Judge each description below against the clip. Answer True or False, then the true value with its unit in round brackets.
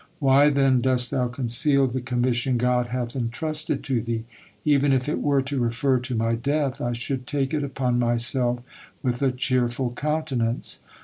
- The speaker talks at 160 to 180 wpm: True (170 wpm)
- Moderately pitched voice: False (125 Hz)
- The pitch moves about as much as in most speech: False (2.3 semitones)